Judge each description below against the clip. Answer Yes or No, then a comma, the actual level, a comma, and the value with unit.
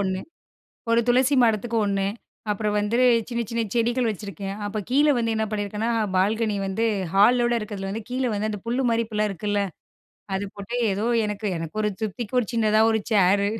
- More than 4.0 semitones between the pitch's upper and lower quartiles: No, narrow, 2.5 semitones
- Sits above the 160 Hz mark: Yes, high, 215 Hz